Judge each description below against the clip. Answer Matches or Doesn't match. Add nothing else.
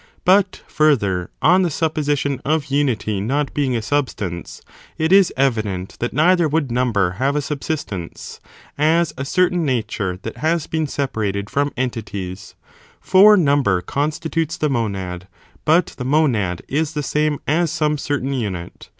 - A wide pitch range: Matches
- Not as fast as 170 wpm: Matches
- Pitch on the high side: Doesn't match